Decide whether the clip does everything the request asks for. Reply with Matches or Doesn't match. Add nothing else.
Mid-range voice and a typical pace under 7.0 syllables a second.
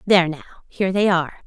Doesn't match